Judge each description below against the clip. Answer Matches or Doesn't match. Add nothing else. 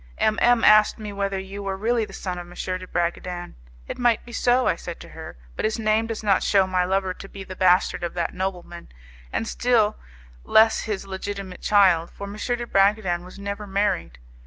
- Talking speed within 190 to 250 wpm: Matches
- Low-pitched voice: Doesn't match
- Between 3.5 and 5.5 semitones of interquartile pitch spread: Doesn't match